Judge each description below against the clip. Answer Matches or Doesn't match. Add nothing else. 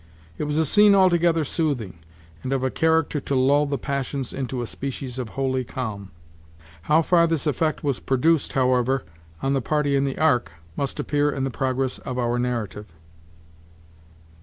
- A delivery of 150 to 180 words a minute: Matches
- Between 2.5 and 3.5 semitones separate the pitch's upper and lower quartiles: Matches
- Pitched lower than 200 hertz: Matches